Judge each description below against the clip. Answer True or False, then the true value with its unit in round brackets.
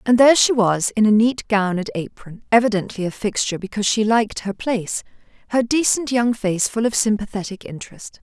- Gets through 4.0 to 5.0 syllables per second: False (5.8 syllables/s)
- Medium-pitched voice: False (220 Hz)